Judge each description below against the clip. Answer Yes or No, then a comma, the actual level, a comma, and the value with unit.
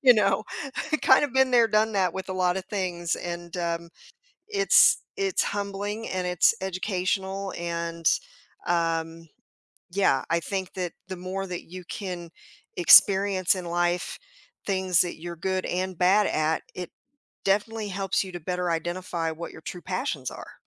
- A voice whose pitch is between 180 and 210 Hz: Yes, medium, 185 Hz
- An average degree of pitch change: No, narrow, 2.3 semitones